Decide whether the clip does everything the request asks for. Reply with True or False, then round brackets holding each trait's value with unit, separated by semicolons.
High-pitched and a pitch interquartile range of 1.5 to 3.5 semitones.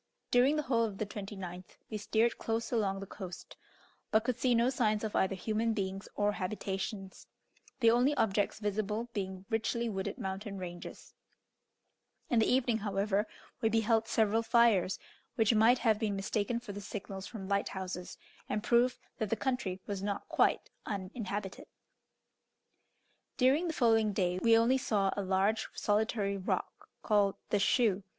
True (210 Hz; 2.8 semitones)